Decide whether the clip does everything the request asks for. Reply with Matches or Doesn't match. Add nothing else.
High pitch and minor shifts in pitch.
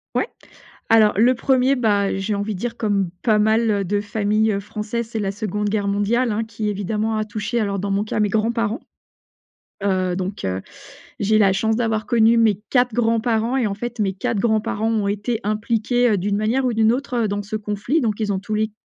Matches